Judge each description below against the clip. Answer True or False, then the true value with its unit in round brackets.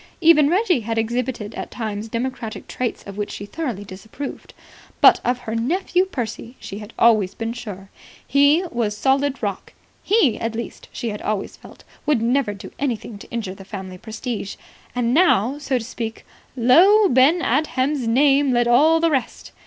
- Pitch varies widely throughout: False (4.5 semitones)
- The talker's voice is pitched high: True (240 Hz)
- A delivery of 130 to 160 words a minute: False (170 wpm)